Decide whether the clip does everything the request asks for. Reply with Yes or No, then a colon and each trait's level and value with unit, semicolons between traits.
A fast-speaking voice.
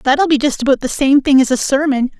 Yes: fast, 300 wpm